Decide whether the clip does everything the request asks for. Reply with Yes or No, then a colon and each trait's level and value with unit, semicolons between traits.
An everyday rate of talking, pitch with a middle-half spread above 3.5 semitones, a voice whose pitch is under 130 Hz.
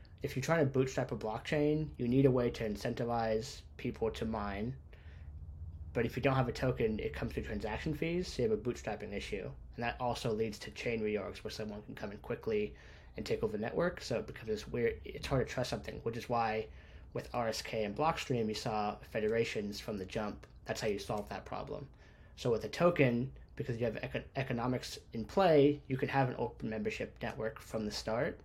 No: fast, 210 wpm; average, 3.9 semitones; low, 115 Hz